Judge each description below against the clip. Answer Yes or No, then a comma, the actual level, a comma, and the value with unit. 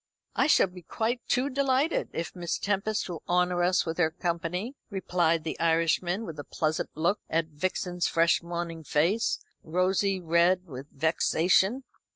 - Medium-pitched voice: Yes, medium, 175 Hz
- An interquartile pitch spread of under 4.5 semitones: Yes, average, 2.7 semitones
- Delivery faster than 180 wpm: No, average, 155 wpm